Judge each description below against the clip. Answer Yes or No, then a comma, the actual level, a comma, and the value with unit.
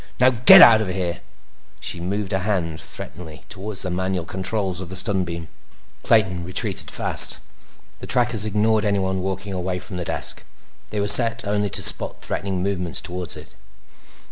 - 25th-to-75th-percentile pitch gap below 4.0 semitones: Yes, narrow, 2.5 semitones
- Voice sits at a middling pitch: No, very low, 95 Hz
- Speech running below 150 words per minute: No, average, 170 wpm